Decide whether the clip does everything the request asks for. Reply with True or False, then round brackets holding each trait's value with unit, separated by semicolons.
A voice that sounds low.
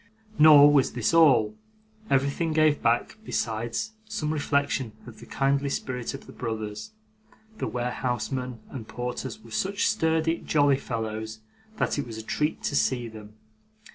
True (130 Hz)